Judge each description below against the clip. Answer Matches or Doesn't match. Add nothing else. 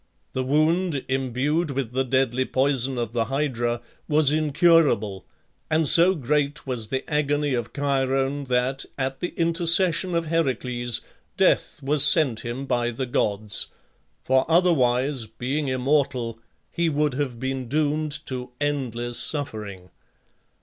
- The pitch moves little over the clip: Doesn't match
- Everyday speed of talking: Doesn't match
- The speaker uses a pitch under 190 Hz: Matches